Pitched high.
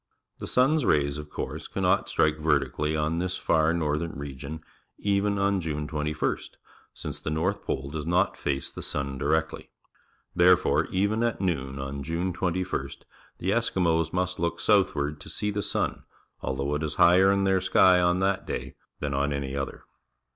No: very low, 80 Hz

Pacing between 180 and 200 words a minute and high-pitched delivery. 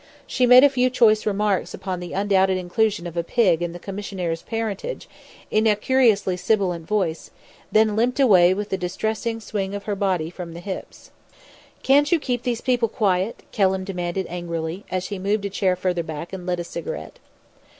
Yes: average, 185 wpm; high, 195 Hz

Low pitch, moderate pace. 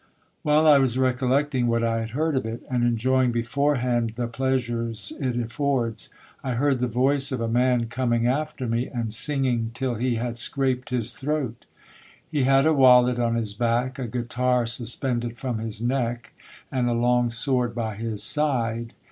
Yes: low, 125 Hz; average, 180 wpm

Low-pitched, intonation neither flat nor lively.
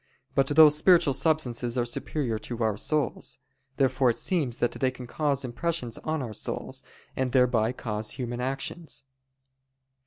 Yes: low, 130 Hz; average, 3.8 semitones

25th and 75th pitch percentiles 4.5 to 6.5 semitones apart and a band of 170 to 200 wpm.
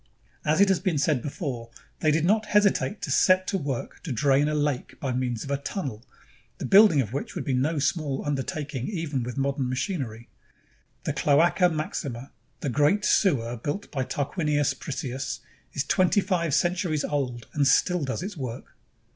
Yes: average, 4.9 semitones; average, 175 wpm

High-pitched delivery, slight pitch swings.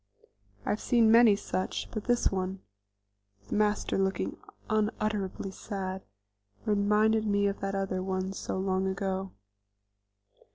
Yes: high, 195 Hz; narrow, 2.0 semitones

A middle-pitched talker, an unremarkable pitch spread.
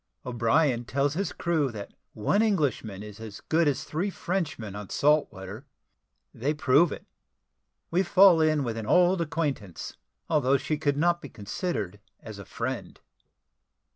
No: medium, 145 Hz; wide, 6.9 semitones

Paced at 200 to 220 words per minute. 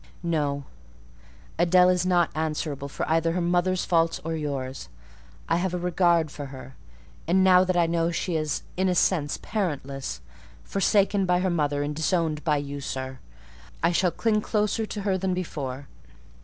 No: average, 160 wpm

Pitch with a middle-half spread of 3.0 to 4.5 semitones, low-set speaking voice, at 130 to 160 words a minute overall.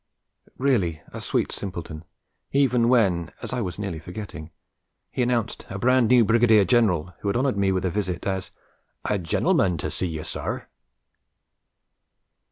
No: average, 5.1 semitones; low, 100 Hz; average, 155 wpm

